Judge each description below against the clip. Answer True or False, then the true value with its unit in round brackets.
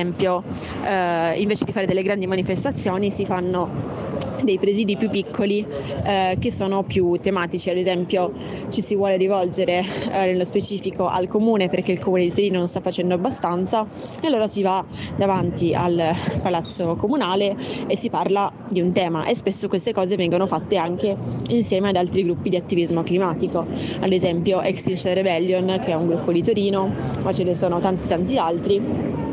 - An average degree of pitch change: False (1.9 semitones)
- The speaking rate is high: True (175 wpm)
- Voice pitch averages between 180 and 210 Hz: True (185 Hz)